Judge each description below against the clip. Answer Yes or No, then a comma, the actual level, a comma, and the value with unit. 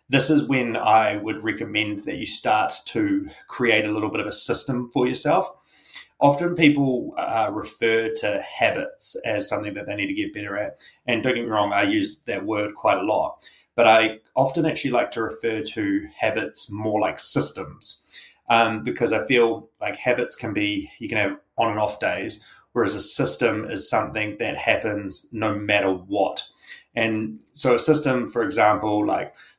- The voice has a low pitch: Yes, low, 120 Hz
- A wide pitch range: Yes, wide, 5.8 semitones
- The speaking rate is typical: Yes, average, 185 wpm